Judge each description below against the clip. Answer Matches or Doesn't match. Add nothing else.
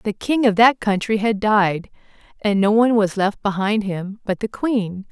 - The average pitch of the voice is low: Doesn't match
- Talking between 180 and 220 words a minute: Matches